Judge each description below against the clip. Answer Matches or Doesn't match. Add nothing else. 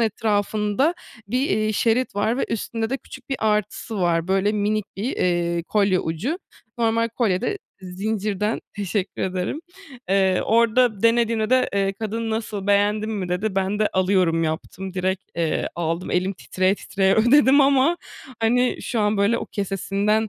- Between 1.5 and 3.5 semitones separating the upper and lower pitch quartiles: Matches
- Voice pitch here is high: Matches